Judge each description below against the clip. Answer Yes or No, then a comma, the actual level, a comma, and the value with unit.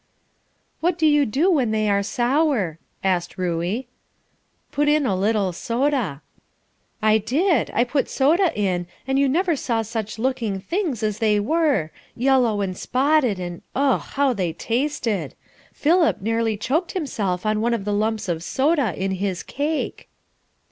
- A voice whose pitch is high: Yes, high, 230 Hz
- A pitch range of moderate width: No, wide, 6.2 semitones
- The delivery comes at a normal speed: Yes, average, 155 wpm